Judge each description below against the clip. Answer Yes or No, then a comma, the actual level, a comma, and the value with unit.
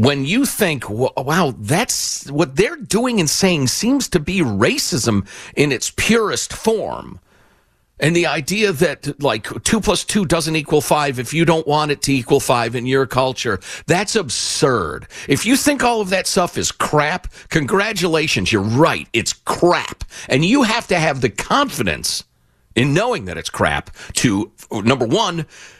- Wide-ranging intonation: Yes, wide, 5.7 semitones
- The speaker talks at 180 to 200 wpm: No, average, 165 wpm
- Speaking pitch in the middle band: Yes, medium, 155 Hz